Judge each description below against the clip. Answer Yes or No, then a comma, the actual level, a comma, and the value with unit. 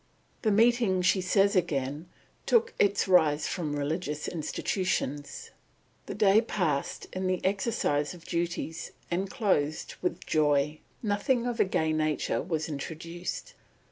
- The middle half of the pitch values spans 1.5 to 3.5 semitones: No, average, 4.7 semitones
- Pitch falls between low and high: Yes, medium, 175 Hz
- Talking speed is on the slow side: Yes, slow, 130 wpm